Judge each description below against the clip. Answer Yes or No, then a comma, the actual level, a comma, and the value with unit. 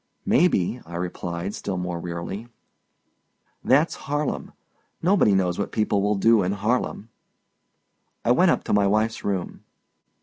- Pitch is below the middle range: Yes, low, 100 Hz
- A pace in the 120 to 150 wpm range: Yes, average, 140 wpm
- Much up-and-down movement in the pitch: No, average, 4.2 semitones